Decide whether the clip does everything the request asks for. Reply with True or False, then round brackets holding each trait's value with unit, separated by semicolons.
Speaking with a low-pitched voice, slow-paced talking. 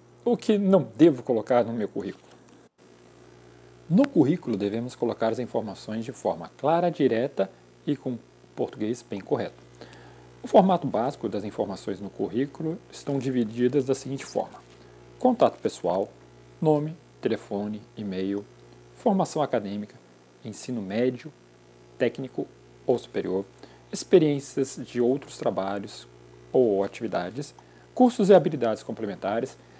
True (105 Hz; 115 wpm)